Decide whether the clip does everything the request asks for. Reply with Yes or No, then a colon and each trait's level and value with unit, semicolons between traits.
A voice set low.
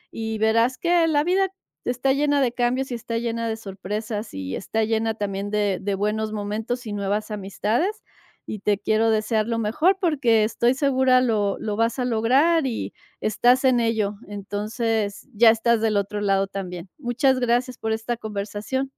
No: high, 225 Hz